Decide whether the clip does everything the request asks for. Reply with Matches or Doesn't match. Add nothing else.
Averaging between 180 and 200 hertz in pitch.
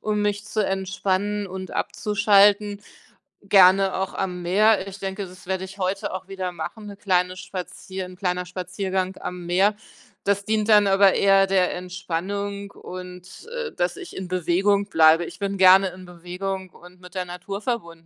Matches